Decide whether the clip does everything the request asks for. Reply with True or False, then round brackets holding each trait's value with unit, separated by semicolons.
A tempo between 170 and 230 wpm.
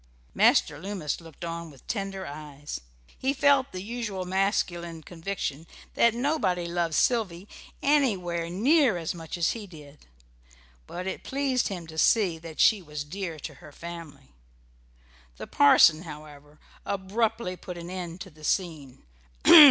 False (145 wpm)